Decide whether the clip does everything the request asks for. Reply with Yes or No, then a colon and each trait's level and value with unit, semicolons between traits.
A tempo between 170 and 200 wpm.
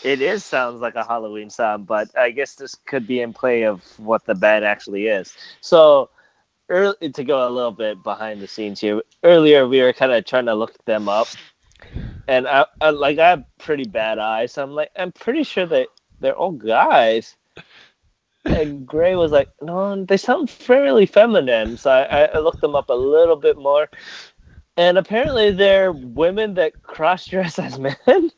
Yes: average, 190 wpm